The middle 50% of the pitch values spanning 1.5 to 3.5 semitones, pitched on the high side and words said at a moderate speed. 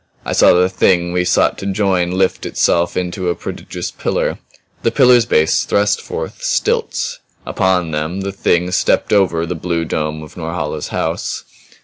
No: average, 3.0 semitones; very low, 90 Hz; average, 160 wpm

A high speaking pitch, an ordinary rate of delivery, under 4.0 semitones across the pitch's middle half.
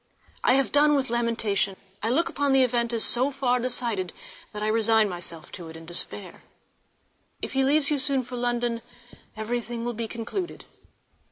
Yes: high, 240 Hz; average, 175 wpm; average, 3.4 semitones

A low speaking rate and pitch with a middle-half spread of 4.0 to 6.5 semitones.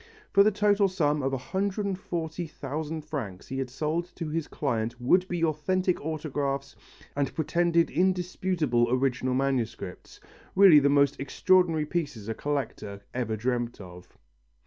Yes: slow, 130 wpm; average, 5.3 semitones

